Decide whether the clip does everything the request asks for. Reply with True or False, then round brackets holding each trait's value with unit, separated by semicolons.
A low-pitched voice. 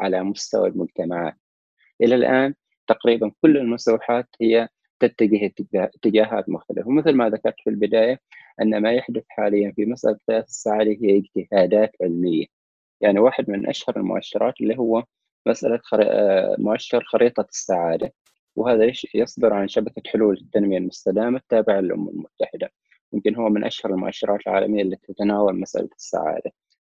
True (105 Hz)